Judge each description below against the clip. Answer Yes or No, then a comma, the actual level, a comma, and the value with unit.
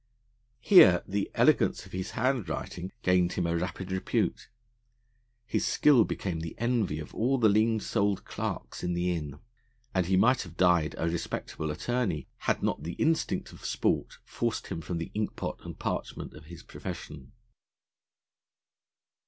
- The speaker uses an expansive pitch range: No, average, 4.8 semitones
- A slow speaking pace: No, average, 155 wpm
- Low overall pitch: Yes, very low, 90 Hz